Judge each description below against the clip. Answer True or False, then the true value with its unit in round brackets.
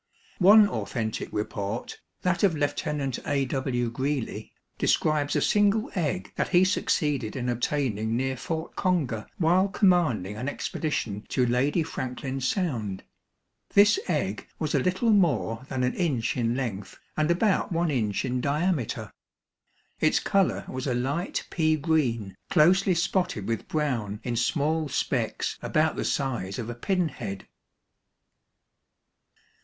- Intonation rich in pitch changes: True (6.2 semitones)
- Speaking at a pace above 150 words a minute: False (135 wpm)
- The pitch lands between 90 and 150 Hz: True (140 Hz)